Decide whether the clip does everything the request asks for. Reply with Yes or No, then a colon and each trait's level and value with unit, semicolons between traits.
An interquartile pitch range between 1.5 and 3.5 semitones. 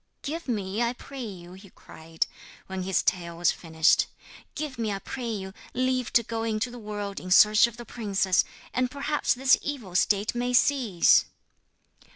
No: average, 4.5 semitones